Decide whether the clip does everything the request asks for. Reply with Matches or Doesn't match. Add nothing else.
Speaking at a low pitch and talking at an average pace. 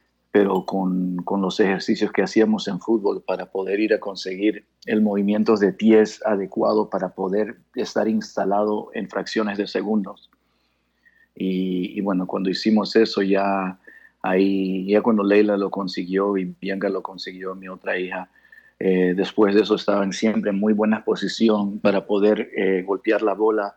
Matches